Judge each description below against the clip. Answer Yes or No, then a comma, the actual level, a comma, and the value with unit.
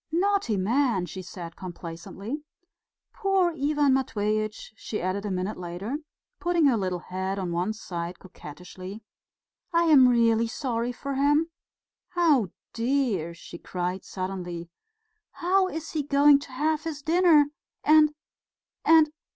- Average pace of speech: No, slow, 130 wpm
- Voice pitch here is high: Yes, high, 230 Hz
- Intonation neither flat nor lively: No, wide, 8.2 semitones